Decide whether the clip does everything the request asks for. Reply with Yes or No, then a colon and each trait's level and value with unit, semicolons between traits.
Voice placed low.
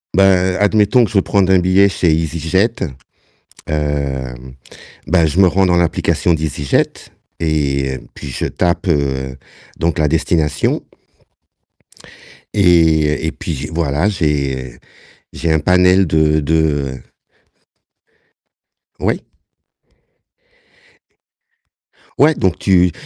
Yes: very low, 80 Hz